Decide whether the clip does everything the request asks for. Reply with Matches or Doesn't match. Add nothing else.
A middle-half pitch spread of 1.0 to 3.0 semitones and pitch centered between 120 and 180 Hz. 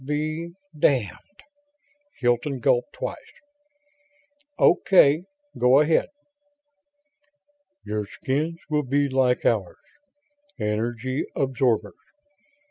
Doesn't match